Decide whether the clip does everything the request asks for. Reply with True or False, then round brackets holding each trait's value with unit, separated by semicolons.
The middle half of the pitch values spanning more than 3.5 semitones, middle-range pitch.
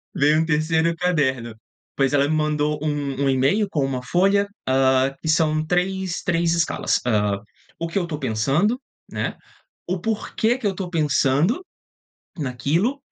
True (4.7 semitones; 155 Hz)